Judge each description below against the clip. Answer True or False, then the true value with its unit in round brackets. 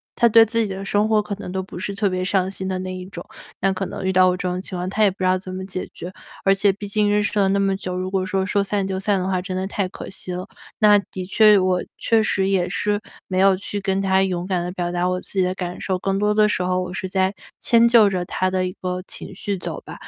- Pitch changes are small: True (1.6 semitones)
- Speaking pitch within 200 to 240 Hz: False (190 Hz)